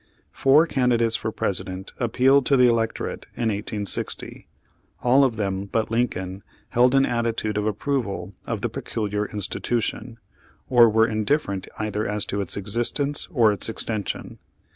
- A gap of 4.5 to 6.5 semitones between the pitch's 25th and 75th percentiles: No, average, 3.1 semitones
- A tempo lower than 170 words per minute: Yes, average, 140 wpm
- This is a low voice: Yes, low, 110 Hz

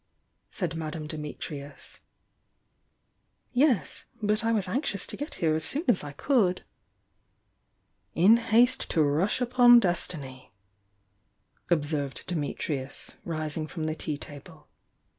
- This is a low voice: No, medium, 165 Hz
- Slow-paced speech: Yes, slow, 120 wpm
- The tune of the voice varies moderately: No, wide, 6.9 semitones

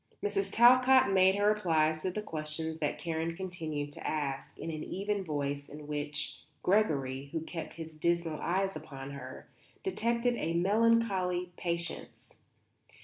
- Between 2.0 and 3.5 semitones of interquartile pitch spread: No, average, 4.5 semitones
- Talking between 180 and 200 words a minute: No, average, 145 wpm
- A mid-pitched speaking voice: Yes, medium, 170 Hz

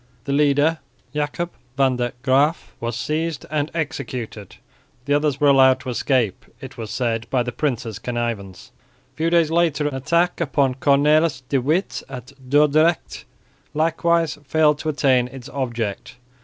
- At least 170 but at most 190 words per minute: No, average, 150 wpm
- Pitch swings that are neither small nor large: Yes, average, 3.7 semitones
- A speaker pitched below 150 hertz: Yes, medium, 140 Hz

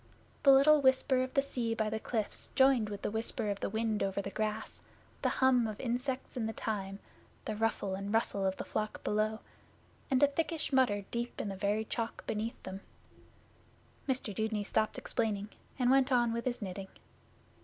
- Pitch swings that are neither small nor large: Yes, average, 3.5 semitones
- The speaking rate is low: No, average, 185 wpm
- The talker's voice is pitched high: Yes, high, 225 Hz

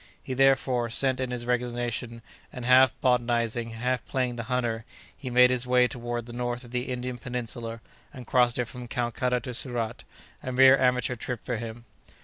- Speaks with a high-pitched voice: No, low, 125 Hz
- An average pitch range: No, narrow, 1.1 semitones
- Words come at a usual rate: Yes, average, 175 wpm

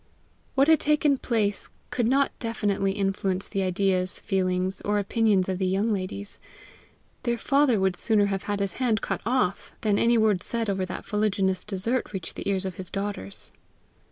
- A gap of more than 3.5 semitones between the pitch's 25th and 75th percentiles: No, average, 3.2 semitones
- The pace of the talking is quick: No, average, 175 wpm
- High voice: Yes, high, 200 Hz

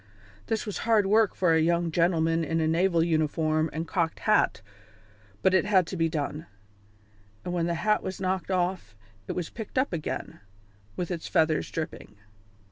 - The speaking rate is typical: Yes, average, 175 wpm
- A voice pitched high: No, medium, 170 Hz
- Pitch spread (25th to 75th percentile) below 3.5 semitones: Yes, average, 2.7 semitones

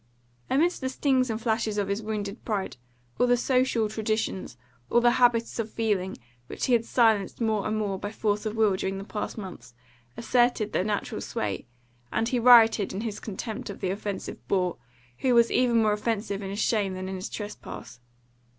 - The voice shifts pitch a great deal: No, average, 2.9 semitones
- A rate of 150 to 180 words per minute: No, average, 190 wpm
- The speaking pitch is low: No, high, 215 Hz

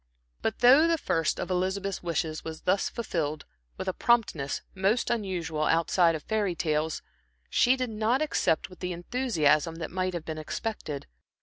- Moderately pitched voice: Yes, medium, 180 Hz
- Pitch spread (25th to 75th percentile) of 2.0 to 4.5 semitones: No, wide, 5.4 semitones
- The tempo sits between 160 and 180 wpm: Yes, average, 165 wpm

